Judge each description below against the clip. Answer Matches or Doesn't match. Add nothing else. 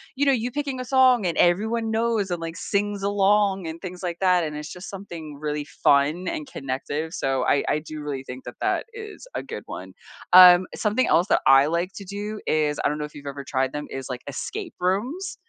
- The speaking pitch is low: Doesn't match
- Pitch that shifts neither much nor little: Doesn't match